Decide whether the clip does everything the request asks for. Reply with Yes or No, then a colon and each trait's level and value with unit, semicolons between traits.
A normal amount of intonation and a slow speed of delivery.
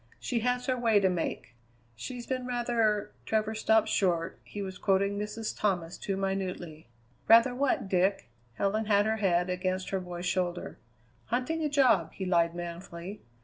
No: average, 3.8 semitones; average, 165 wpm